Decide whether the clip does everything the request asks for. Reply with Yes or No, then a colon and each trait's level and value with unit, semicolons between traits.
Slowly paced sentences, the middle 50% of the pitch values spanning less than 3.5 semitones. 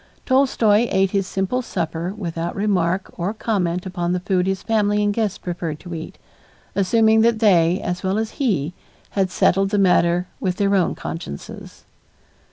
No: average, 165 wpm; average, 3.0 semitones